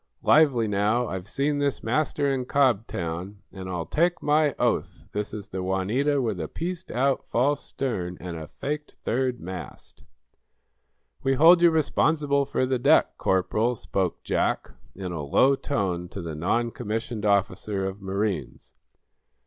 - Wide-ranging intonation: Yes, wide, 6.6 semitones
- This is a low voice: Yes, low, 115 Hz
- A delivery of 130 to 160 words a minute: Yes, average, 150 wpm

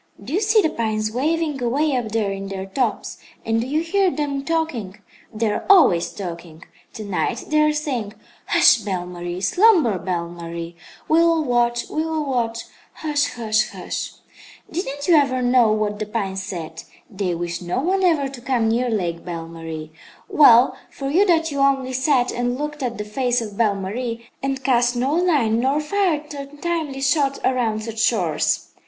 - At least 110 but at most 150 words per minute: No, average, 180 wpm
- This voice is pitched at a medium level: No, high, 245 Hz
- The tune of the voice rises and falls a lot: Yes, wide, 6.1 semitones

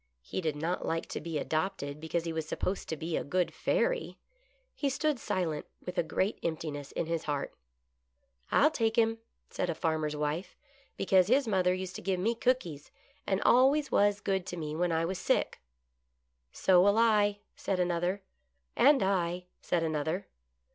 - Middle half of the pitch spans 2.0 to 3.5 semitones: No, average, 4.4 semitones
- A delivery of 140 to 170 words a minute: No, average, 185 wpm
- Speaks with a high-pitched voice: No, medium, 180 Hz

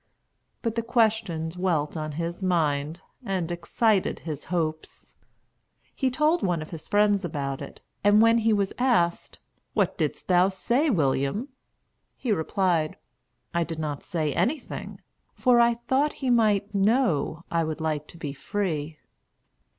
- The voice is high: No, medium, 180 Hz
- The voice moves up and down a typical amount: No, wide, 6.1 semitones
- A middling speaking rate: Yes, average, 145 wpm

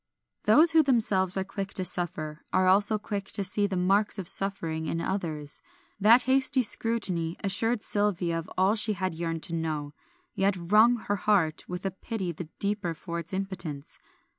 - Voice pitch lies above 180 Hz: Yes, high, 190 Hz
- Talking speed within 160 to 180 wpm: Yes, average, 175 wpm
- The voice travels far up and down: No, average, 3.6 semitones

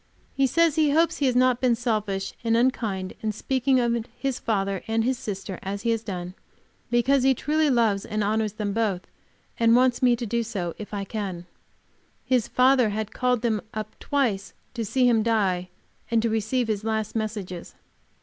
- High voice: Yes, high, 225 Hz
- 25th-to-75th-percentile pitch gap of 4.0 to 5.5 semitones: No, average, 3.5 semitones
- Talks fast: No, average, 185 wpm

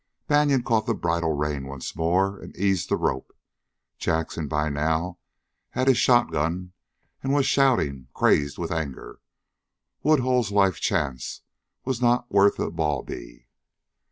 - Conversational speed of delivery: No, slow, 130 wpm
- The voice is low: Yes, very low, 90 Hz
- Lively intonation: Yes, wide, 8.2 semitones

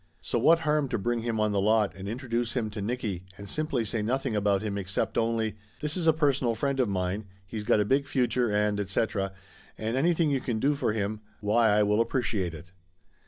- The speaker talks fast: Yes, fast, 220 wpm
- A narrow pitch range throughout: No, average, 4.0 semitones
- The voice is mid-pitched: No, low, 110 Hz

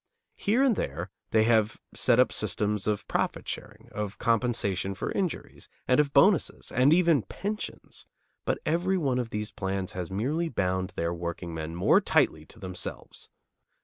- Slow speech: No, average, 155 wpm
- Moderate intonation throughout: No, wide, 7.7 semitones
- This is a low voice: Yes, low, 105 Hz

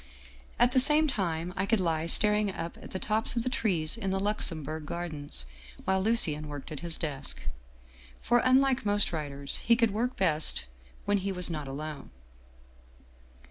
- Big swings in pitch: Yes, wide, 6.1 semitones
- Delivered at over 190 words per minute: No, average, 175 wpm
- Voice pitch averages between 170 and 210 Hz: Yes, high, 190 Hz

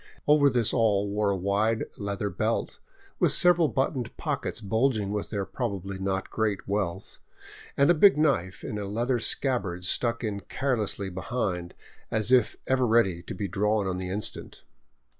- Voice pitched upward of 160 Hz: No, low, 105 Hz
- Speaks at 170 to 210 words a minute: No, average, 160 wpm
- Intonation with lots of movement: No, average, 3.9 semitones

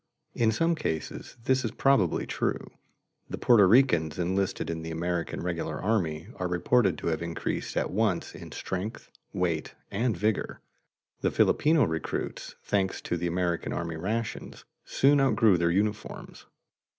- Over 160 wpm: No, average, 145 wpm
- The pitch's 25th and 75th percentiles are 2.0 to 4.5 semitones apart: No, average, 5.1 semitones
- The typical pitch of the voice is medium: No, very low, 95 Hz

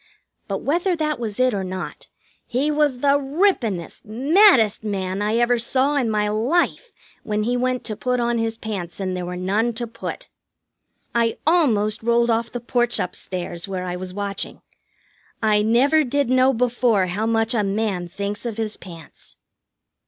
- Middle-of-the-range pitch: No, high, 225 Hz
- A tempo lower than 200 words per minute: Yes, average, 175 wpm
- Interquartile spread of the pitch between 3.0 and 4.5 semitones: Yes, average, 3.9 semitones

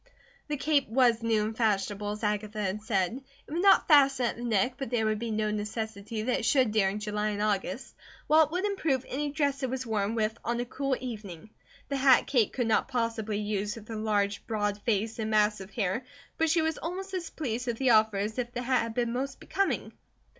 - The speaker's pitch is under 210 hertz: No, high, 225 Hz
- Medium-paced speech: No, fast, 225 wpm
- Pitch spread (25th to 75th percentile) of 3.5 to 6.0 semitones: Yes, average, 3.9 semitones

